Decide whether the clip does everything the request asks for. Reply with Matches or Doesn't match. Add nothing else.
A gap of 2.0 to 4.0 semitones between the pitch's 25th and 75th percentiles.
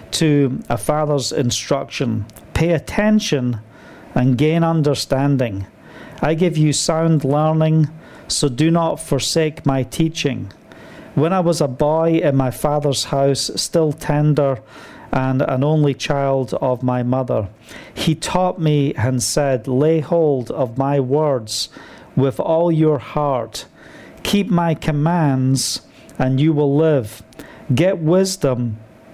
Matches